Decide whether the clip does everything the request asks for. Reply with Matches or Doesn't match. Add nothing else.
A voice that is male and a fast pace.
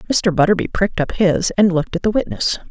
Doesn't match